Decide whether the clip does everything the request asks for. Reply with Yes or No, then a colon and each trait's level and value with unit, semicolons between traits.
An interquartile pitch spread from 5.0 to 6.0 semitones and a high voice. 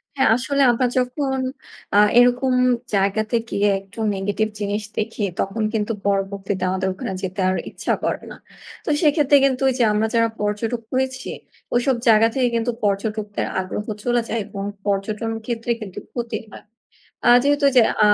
No: average, 3.7 semitones; high, 220 Hz